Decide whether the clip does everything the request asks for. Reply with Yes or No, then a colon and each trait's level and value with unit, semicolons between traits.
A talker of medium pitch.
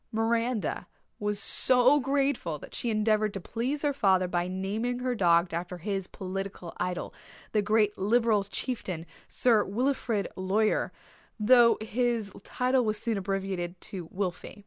No: high, 210 Hz